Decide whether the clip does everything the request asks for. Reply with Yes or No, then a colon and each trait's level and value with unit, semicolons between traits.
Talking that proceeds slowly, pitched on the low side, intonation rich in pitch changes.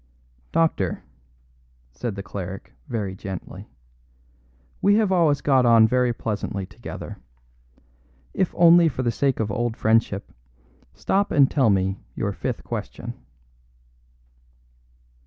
Yes: slow, 115 wpm; low, 120 Hz; wide, 6.7 semitones